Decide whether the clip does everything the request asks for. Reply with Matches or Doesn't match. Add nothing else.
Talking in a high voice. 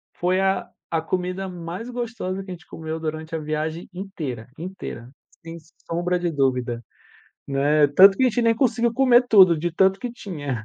Doesn't match